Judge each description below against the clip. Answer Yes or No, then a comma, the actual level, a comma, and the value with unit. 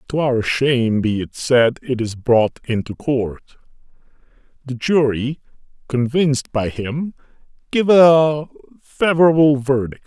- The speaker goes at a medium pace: No, slow, 120 wpm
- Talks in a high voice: No, low, 135 Hz